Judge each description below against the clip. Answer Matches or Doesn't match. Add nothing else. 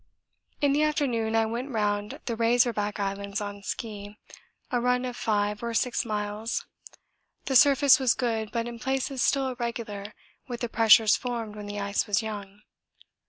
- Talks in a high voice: Matches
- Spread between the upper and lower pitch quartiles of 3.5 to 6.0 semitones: Doesn't match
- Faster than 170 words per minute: Doesn't match